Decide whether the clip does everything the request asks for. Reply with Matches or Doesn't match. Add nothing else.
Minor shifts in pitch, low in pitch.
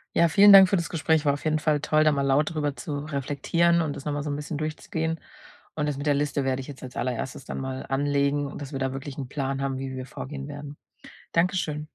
Doesn't match